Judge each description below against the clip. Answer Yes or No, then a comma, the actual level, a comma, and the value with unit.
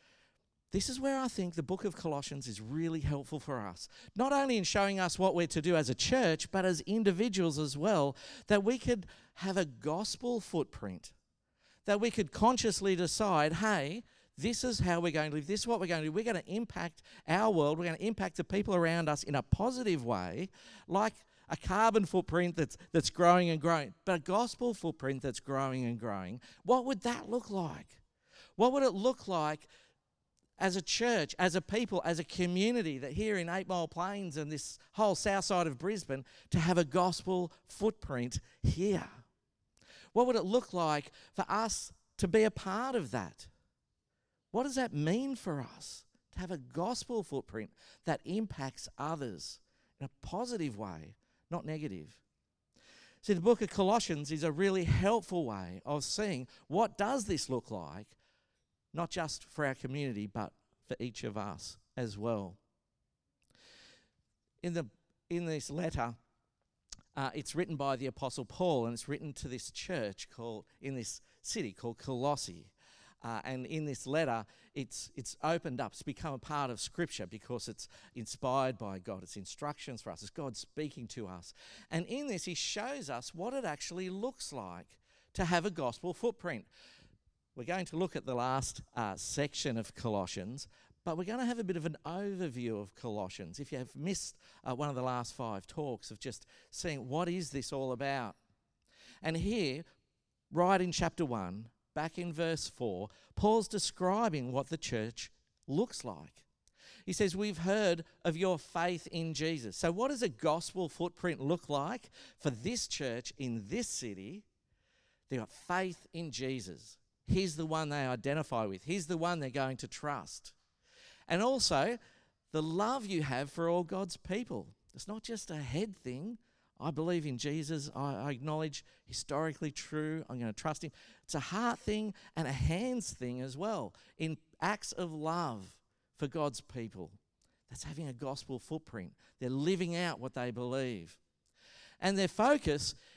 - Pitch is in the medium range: Yes, medium, 160 Hz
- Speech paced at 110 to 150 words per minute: No, average, 175 wpm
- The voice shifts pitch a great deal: Yes, wide, 6.6 semitones